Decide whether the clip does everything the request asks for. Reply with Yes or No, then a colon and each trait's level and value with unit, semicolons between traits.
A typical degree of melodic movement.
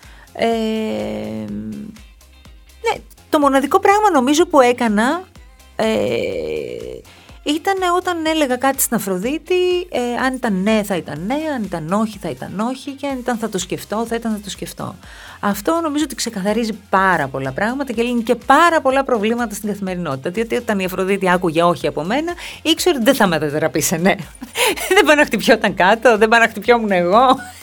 No: wide, 7.3 semitones